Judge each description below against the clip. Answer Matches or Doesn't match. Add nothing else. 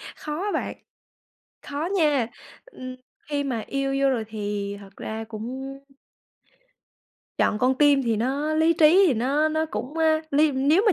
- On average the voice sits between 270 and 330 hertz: Matches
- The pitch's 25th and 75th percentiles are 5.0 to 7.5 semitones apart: Doesn't match